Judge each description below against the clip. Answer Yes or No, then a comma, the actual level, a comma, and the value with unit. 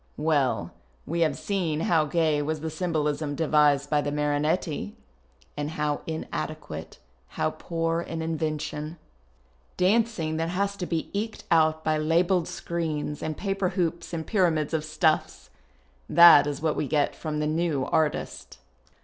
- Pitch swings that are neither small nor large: No, narrow, 2.1 semitones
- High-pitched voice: No, medium, 160 Hz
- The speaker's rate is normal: Yes, average, 145 wpm